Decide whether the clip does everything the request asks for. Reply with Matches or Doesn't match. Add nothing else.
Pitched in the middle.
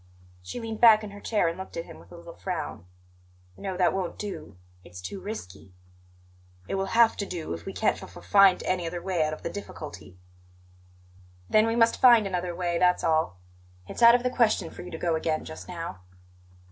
Matches